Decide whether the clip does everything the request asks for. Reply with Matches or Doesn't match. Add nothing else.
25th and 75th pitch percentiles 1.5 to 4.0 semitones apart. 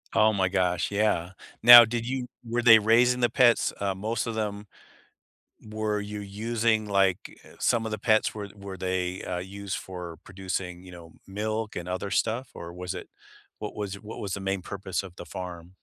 Matches